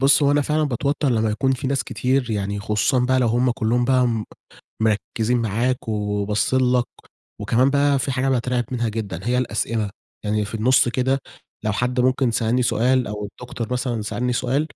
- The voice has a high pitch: No, low, 125 Hz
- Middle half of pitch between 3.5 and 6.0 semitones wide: No, average, 2.7 semitones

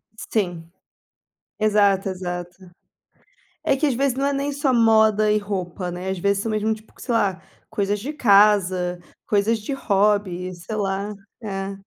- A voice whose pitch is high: Yes, high, 205 Hz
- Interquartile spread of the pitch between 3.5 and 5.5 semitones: No, average, 2.8 semitones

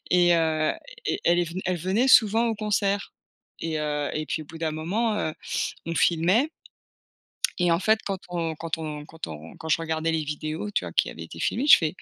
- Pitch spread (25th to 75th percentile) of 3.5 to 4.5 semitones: Yes, average, 4.1 semitones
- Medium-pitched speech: Yes, medium, 165 Hz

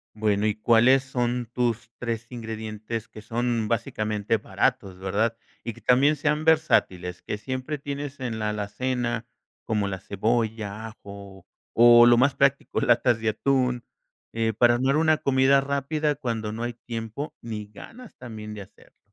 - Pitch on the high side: No, low, 115 Hz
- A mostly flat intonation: No, average, 3.4 semitones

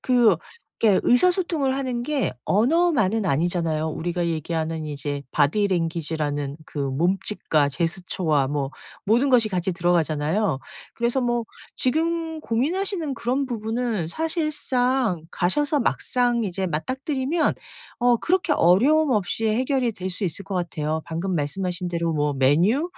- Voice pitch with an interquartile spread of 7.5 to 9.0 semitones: Yes, wide, 7.9 semitones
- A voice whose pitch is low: No, high, 200 Hz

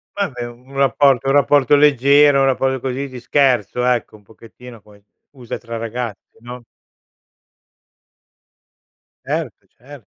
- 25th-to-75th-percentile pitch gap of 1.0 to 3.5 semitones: Yes, narrow, 2.6 semitones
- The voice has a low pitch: Yes, low, 125 Hz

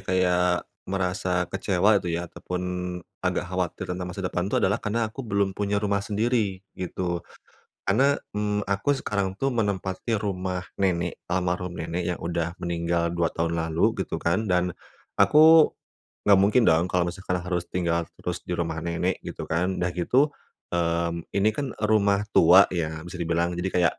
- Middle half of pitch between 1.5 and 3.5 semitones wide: Yes, narrow, 2.6 semitones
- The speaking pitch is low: Yes, very low, 90 Hz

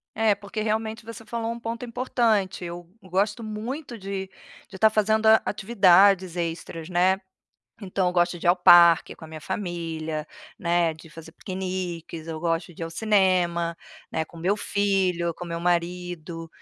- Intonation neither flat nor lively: Yes, average, 3.8 semitones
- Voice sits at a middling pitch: Yes, medium, 180 Hz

